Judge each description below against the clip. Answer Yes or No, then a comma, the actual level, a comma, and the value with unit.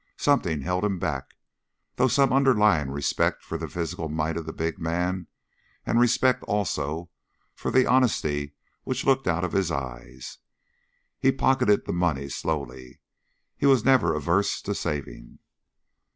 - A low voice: Yes, very low, 85 Hz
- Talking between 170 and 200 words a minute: No, average, 150 wpm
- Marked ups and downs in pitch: Yes, wide, 8.6 semitones